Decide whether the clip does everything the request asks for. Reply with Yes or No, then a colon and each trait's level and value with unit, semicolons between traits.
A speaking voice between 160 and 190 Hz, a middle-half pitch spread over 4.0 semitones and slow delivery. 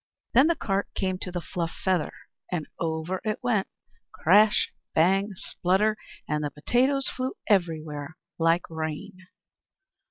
Yes: medium, 185 Hz; average, 4.6 semitones; slow, 130 wpm